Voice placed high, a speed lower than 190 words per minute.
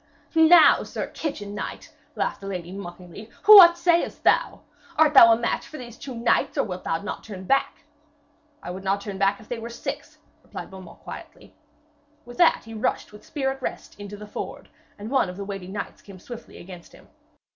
No: high, 210 Hz; average, 195 wpm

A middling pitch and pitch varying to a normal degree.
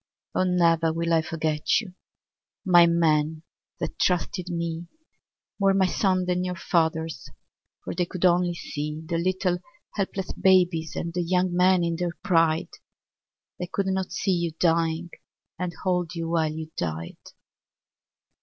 No: medium, 170 Hz; narrow, 1.9 semitones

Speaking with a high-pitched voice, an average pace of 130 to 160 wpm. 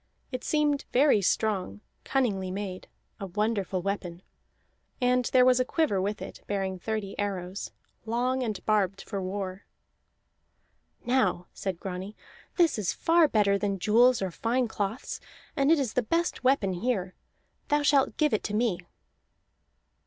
Yes: high, 210 Hz; average, 145 wpm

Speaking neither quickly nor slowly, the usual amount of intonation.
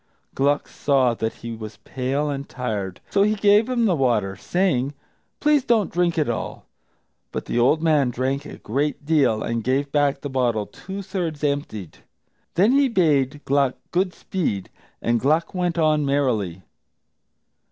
No: average, 160 wpm; wide, 6.0 semitones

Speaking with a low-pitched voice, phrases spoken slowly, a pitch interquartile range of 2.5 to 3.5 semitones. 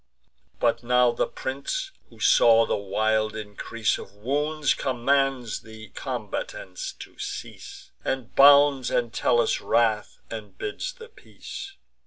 No: low, 120 Hz; slow, 120 wpm; average, 4.4 semitones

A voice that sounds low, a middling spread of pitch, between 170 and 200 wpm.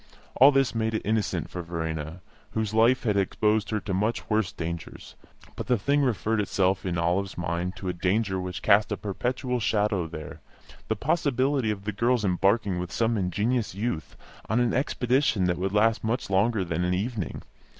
Yes: low, 105 Hz; average, 4.1 semitones; average, 180 wpm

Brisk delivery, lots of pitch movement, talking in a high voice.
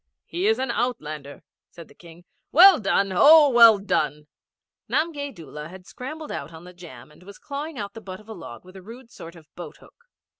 Yes: fast, 210 wpm; wide, 8.3 semitones; high, 200 Hz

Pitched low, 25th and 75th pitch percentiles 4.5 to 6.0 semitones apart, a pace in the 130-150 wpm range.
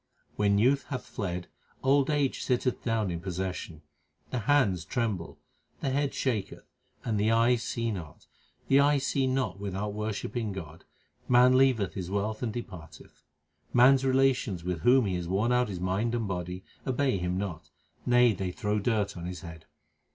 No: low, 105 Hz; average, 5.3 semitones; average, 175 wpm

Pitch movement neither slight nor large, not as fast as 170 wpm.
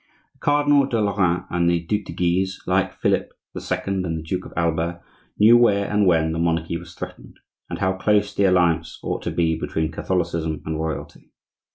No: average, 3.5 semitones; average, 195 wpm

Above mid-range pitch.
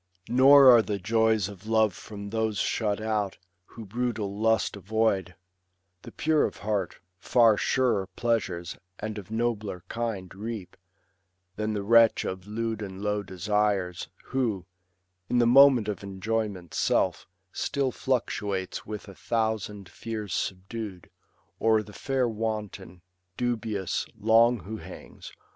No: low, 110 Hz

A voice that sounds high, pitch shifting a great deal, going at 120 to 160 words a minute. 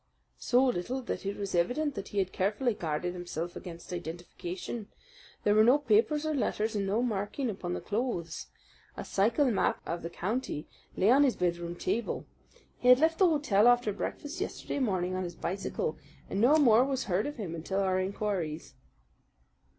No: high, 205 Hz; wide, 5.8 semitones; average, 180 wpm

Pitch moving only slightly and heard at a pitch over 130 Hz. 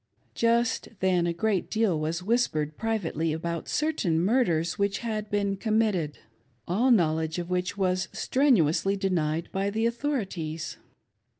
No: average, 5.1 semitones; high, 190 Hz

